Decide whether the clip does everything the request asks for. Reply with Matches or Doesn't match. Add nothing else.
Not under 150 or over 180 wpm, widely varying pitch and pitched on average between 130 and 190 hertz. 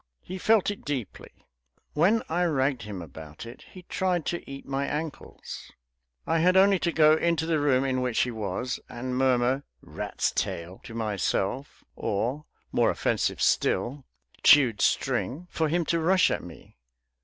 Matches